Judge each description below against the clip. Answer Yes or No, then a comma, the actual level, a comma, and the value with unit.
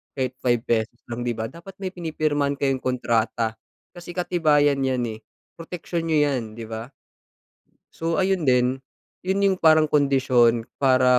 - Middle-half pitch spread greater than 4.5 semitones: Yes, average, 5.1 semitones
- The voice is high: No, low, 135 Hz